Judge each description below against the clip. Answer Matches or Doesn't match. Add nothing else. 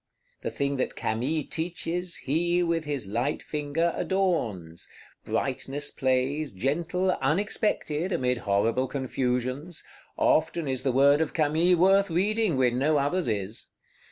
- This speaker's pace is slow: Matches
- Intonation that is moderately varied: Matches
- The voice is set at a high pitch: Doesn't match